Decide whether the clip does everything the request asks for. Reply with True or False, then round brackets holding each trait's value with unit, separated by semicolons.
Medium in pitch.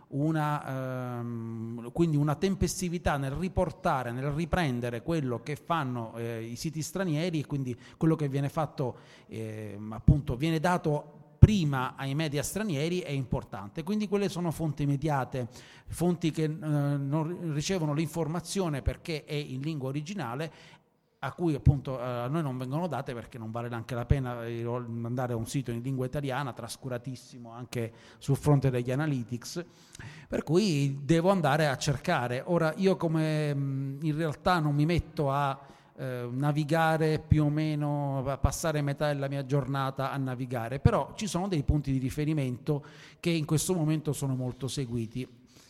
True (145 Hz)